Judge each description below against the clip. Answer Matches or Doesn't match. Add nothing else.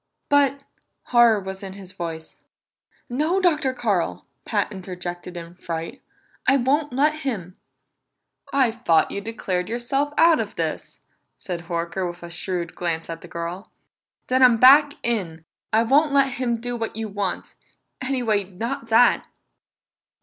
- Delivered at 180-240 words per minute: Doesn't match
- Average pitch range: Doesn't match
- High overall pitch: Matches